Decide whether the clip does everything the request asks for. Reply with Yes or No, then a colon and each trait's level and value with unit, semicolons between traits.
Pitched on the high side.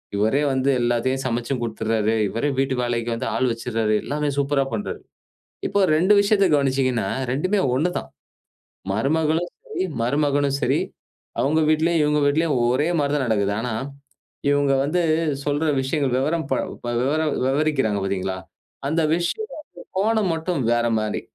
No: medium, 140 Hz